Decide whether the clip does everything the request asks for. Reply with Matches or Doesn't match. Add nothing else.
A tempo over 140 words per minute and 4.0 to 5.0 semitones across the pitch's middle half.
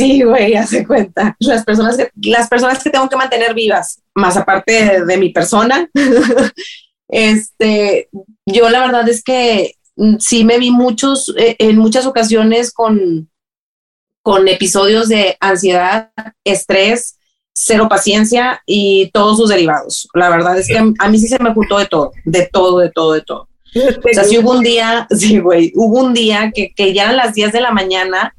Doesn't match